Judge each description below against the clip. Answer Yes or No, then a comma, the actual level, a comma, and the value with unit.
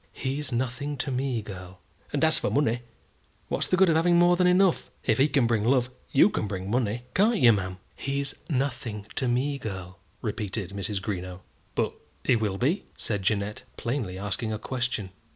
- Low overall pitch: Yes, low, 120 Hz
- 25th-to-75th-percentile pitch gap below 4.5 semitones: No, wide, 5.5 semitones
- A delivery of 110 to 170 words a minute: No, average, 185 wpm